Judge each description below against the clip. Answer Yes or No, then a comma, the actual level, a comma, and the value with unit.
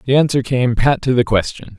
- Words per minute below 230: No, fast, 235 wpm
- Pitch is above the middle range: No, low, 125 Hz